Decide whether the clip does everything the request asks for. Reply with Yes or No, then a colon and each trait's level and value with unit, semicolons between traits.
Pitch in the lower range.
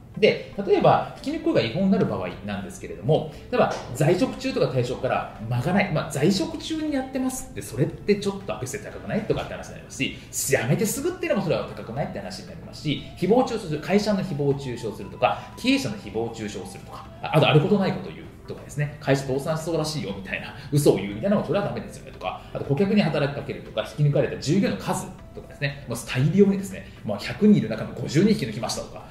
No: medium, 155 Hz